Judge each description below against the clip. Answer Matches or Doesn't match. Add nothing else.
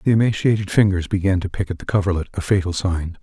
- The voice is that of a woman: Doesn't match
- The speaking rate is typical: Doesn't match